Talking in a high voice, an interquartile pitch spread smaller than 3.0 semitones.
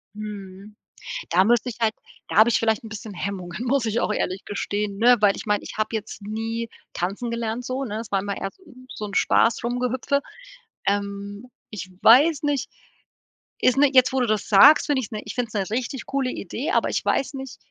No: high, 225 Hz; average, 3.7 semitones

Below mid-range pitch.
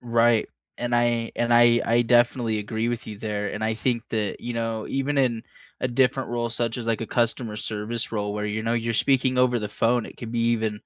Yes: low, 115 Hz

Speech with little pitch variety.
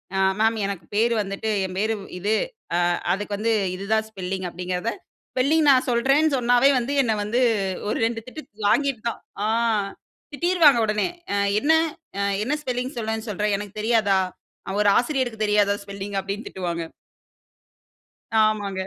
No: average, 3.7 semitones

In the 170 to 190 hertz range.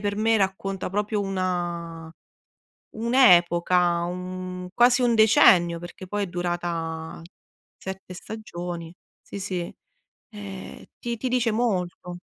Yes: medium, 185 Hz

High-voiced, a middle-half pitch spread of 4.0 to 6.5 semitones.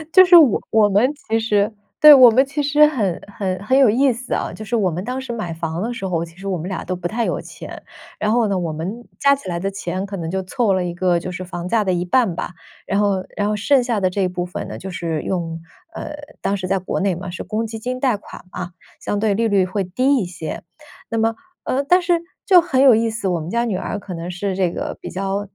Yes: high, 200 Hz; average, 4.7 semitones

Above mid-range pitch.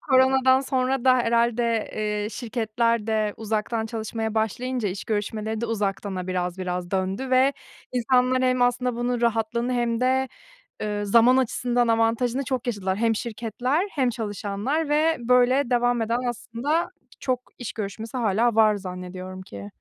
Yes: high, 230 Hz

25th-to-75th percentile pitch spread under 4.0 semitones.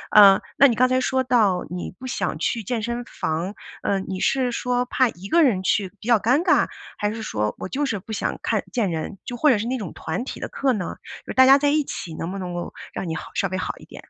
No: average, 5.3 semitones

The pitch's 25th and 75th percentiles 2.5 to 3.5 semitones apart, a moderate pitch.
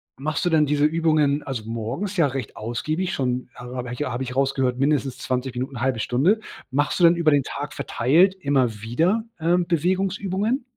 No: average, 5.1 semitones; medium, 145 Hz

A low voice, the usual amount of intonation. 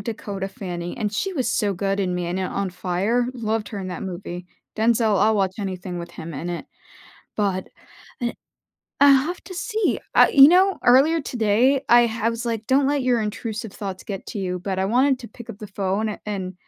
No: high, 210 Hz; average, 4.4 semitones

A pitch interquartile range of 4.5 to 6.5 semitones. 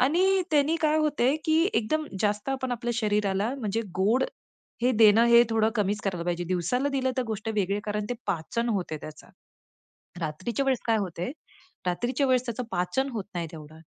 Yes: average, 5.2 semitones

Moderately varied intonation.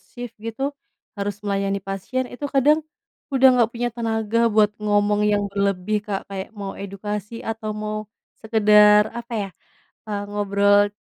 No: narrow, 2.2 semitones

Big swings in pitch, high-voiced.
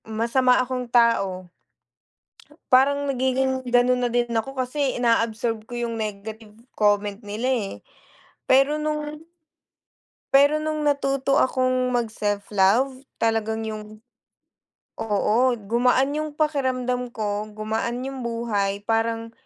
No: average, 3.2 semitones; high, 240 Hz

